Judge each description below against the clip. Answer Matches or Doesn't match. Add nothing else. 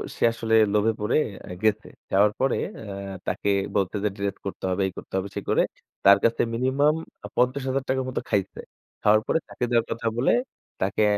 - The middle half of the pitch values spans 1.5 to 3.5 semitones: Doesn't match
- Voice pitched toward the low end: Matches